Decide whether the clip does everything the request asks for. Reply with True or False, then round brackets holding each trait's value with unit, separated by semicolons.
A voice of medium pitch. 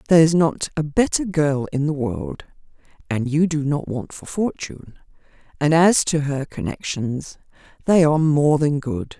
True (150 Hz)